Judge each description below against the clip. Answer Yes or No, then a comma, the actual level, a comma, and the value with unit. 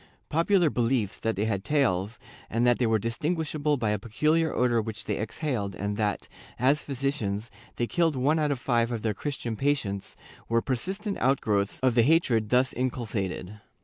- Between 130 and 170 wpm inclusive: No, average, 180 wpm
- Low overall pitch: Yes, low, 120 Hz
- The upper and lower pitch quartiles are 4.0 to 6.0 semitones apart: Yes, average, 5.1 semitones